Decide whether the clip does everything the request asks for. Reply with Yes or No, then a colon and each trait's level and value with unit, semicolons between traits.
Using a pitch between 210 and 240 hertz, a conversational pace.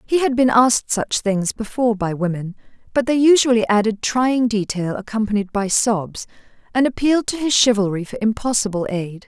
Yes: high, 225 Hz; average, 170 wpm